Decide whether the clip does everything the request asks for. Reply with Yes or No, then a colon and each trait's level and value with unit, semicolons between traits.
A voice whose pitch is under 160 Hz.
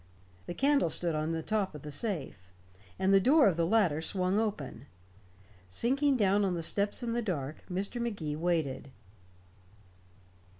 No: medium, 185 Hz